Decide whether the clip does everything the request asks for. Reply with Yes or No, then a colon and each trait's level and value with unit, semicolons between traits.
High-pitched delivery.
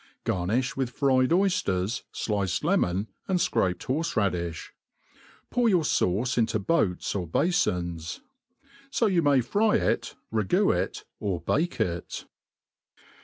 No: low, 115 Hz